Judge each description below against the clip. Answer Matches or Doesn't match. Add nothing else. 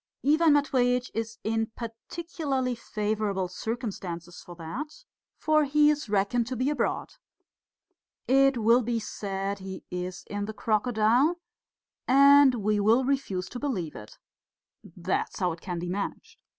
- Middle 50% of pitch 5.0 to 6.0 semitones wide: Matches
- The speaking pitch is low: Doesn't match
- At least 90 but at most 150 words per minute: Matches